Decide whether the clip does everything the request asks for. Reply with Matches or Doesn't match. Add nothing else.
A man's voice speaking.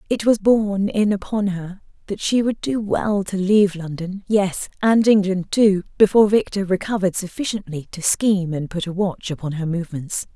Doesn't match